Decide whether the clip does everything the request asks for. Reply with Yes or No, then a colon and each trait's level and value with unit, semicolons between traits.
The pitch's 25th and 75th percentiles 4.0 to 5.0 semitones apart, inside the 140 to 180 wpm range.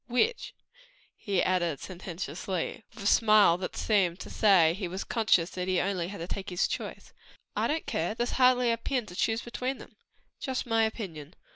No: average, 4.5 semitones; average, 190 wpm